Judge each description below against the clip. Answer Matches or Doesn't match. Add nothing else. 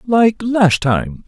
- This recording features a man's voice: Matches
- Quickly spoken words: Doesn't match